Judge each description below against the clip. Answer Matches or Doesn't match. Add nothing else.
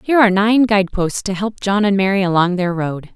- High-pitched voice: Matches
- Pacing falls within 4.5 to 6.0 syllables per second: Matches